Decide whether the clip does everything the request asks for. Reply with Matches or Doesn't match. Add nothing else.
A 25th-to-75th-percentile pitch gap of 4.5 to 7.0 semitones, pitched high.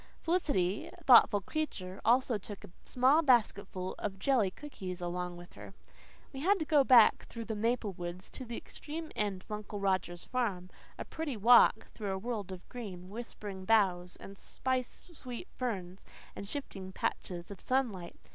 Matches